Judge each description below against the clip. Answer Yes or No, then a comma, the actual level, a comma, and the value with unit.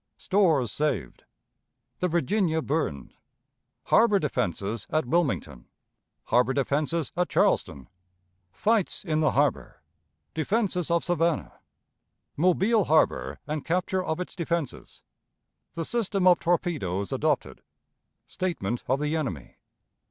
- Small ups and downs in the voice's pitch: No, average, 5.1 semitones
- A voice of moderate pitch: Yes, medium, 160 Hz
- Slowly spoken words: Yes, slow, 105 wpm